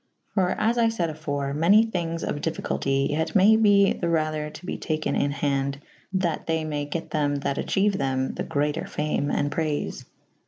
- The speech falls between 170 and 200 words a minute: Yes, average, 190 wpm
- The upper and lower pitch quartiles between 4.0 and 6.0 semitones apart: Yes, average, 4.4 semitones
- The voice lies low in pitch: No, medium, 155 Hz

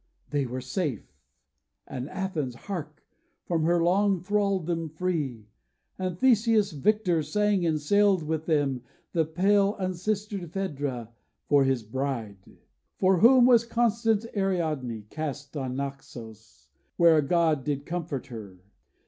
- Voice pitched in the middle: Yes, medium, 165 Hz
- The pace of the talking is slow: Yes, slow, 125 wpm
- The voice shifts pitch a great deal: Yes, wide, 6.0 semitones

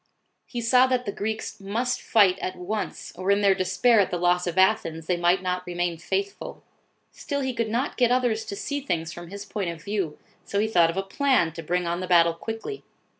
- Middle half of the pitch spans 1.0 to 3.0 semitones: No, average, 4.6 semitones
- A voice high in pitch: Yes, high, 195 Hz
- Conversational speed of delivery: No, fast, 225 wpm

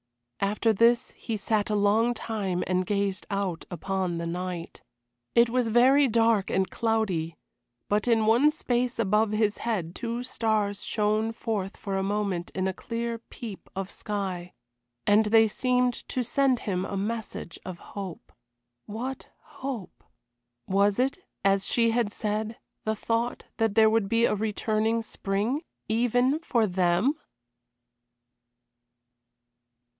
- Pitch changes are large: No, average, 2.9 semitones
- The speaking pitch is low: No, high, 215 Hz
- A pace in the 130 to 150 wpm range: Yes, average, 140 wpm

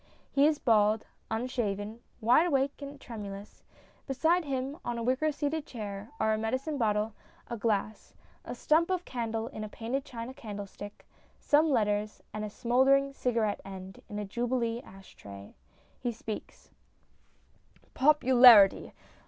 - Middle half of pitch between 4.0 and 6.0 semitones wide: Yes, average, 4.5 semitones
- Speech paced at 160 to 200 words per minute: No, average, 140 wpm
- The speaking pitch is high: Yes, high, 235 Hz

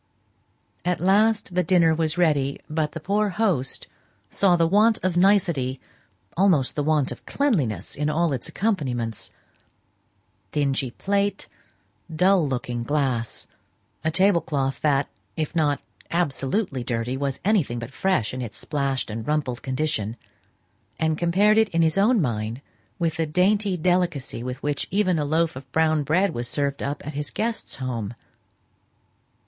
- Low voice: No, medium, 155 Hz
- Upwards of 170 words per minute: No, average, 145 wpm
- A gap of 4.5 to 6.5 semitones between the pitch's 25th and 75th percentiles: Yes, average, 5.3 semitones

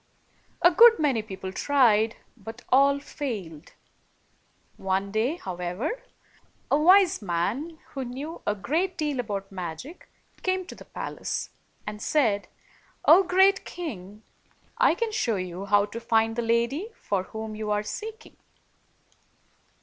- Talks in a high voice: Yes, high, 230 Hz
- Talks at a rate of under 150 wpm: Yes, slow, 135 wpm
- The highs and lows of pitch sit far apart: Yes, wide, 7.6 semitones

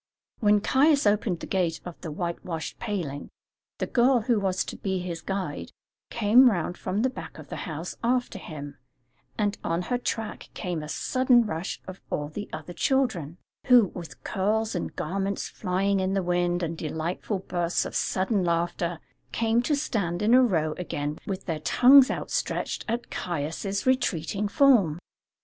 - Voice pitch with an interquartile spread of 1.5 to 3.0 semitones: No, average, 4.8 semitones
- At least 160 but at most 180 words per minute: Yes, average, 165 wpm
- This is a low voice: No, high, 190 Hz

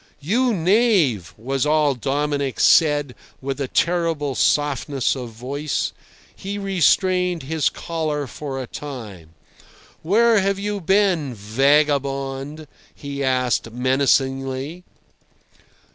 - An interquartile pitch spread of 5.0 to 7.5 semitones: No, average, 4.2 semitones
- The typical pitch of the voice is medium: Yes, medium, 145 Hz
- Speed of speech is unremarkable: No, slow, 100 wpm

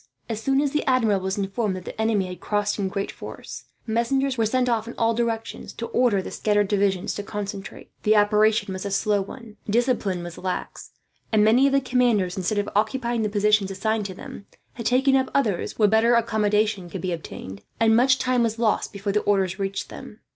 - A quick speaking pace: Yes, fast, 210 wpm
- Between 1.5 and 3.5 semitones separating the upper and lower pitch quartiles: Yes, average, 2.9 semitones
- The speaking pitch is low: No, high, 215 Hz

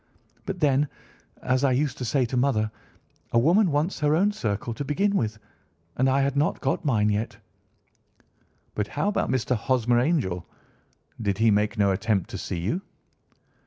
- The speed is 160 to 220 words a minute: Yes, average, 170 wpm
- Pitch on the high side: No, low, 130 Hz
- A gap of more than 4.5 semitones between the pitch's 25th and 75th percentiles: Yes, average, 5.3 semitones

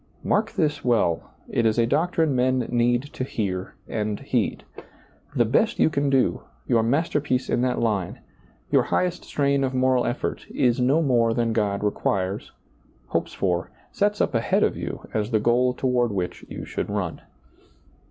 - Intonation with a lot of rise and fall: No, average, 3.8 semitones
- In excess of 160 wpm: Yes, average, 170 wpm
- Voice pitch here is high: No, low, 125 Hz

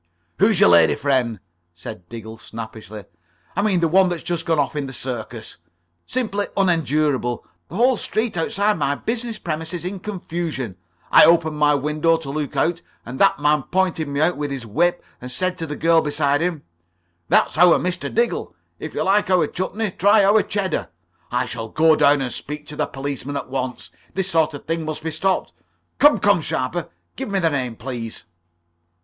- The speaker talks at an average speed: Yes, average, 190 wpm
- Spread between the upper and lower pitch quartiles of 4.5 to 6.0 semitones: Yes, average, 5.0 semitones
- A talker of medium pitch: Yes, medium, 155 Hz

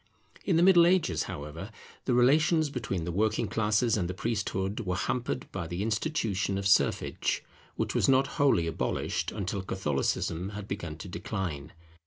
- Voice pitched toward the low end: Yes, low, 100 Hz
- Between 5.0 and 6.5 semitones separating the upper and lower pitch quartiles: Yes, wide, 5.5 semitones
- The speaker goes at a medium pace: Yes, average, 160 wpm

